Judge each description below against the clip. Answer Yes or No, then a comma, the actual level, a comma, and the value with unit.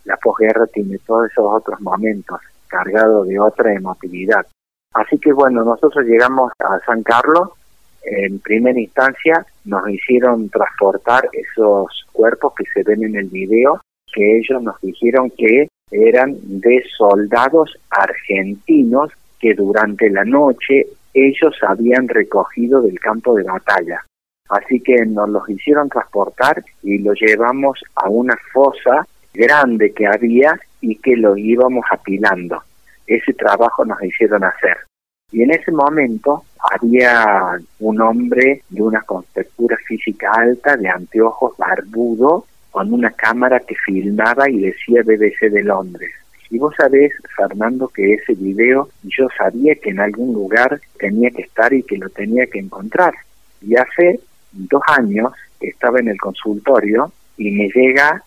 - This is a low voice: Yes, low, 115 Hz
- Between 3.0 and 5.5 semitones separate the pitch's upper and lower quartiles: Yes, average, 4.2 semitones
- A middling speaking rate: Yes, average, 140 wpm